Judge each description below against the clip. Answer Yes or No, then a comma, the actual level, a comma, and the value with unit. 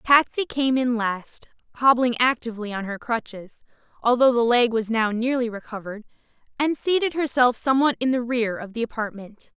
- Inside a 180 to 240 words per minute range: No, average, 165 wpm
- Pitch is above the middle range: Yes, high, 240 Hz